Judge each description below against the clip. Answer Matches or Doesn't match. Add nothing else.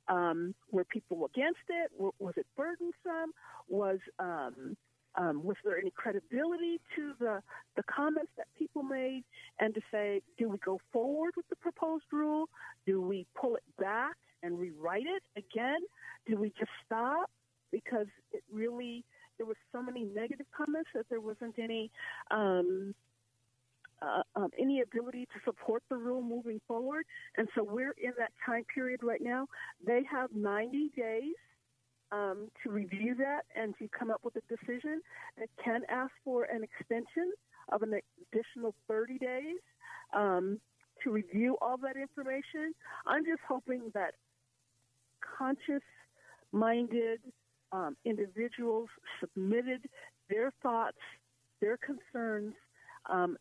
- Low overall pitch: Doesn't match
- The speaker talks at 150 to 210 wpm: Doesn't match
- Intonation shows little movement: Doesn't match